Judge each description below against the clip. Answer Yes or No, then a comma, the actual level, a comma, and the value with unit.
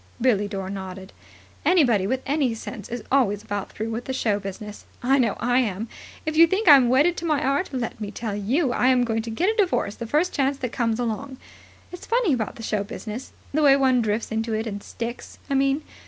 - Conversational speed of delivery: No, fast, 220 wpm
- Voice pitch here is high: Yes, high, 240 Hz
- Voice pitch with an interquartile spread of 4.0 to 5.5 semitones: Yes, average, 4.3 semitones